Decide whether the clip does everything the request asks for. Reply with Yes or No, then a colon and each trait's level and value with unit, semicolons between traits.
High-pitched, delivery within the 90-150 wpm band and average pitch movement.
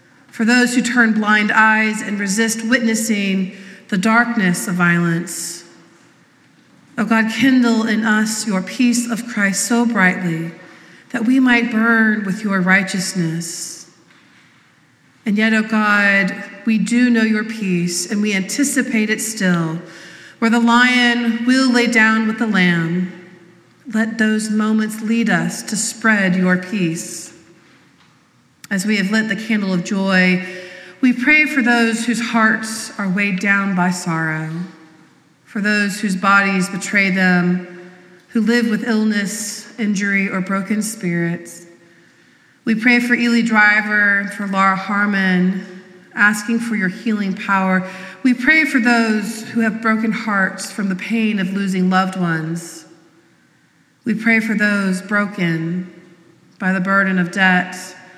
Yes: high, 205 Hz; average, 140 wpm; average, 3.4 semitones